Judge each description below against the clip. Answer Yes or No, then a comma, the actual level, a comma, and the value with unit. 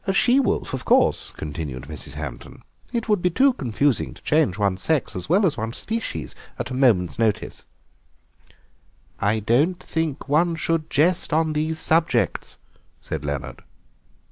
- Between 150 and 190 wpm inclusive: Yes, average, 155 wpm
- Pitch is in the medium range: Yes, medium, 145 Hz